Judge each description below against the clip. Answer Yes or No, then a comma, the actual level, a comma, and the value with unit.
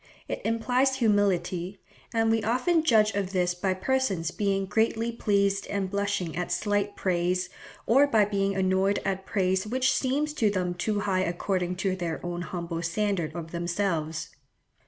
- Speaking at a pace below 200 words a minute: Yes, average, 155 wpm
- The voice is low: No, high, 195 Hz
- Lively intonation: No, average, 3.5 semitones